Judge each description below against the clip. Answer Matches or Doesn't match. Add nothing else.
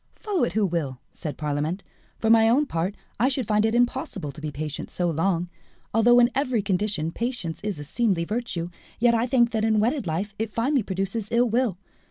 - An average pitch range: Doesn't match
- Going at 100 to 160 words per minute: Doesn't match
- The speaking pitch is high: Matches